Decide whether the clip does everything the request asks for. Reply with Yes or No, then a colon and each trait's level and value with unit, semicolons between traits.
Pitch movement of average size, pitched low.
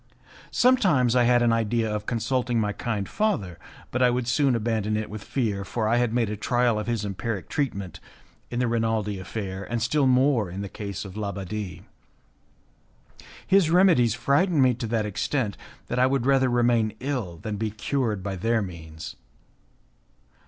Yes: average, 3.3 semitones; low, 115 Hz